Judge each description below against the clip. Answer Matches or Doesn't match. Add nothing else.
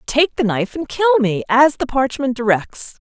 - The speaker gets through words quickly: Doesn't match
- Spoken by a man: Doesn't match